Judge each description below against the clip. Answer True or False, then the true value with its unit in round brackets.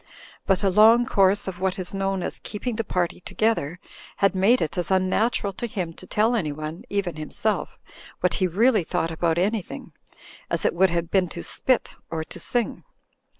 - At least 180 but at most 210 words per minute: True (185 wpm)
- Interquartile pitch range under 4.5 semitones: True (3.6 semitones)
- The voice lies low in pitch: False (190 Hz)